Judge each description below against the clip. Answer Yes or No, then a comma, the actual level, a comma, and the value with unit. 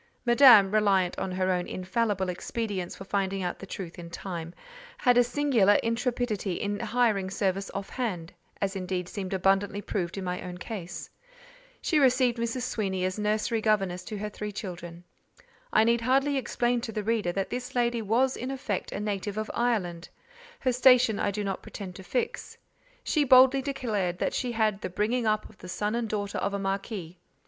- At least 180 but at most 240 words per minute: Yes, average, 185 wpm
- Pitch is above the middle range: Yes, high, 210 Hz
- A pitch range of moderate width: Yes, average, 4.1 semitones